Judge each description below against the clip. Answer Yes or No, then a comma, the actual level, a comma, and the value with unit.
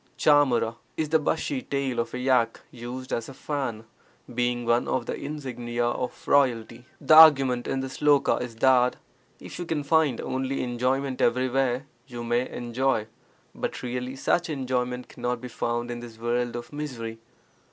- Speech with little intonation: Yes, narrow, 2.2 semitones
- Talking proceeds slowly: No, average, 165 wpm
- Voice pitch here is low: Yes, low, 125 Hz